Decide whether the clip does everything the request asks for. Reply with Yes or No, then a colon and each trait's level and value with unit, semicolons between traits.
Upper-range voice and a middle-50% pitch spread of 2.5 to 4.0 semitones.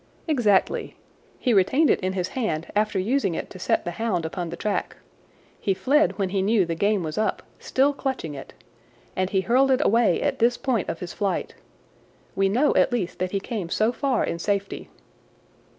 No: high, 200 Hz; average, 4.8 semitones